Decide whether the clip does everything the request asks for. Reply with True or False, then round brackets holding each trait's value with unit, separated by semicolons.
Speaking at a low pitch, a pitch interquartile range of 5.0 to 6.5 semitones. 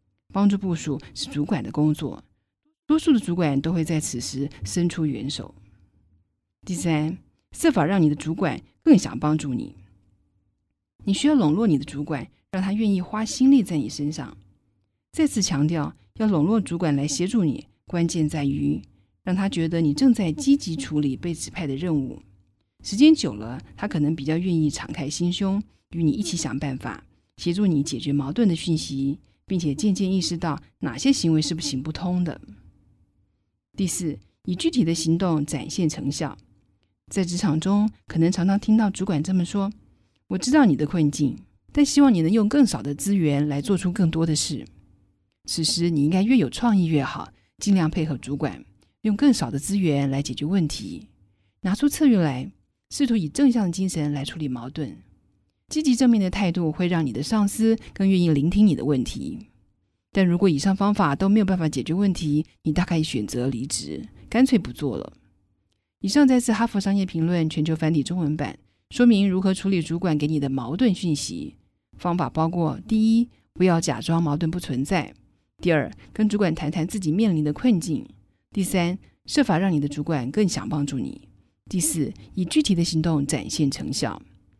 False (160 Hz; 5.4 semitones)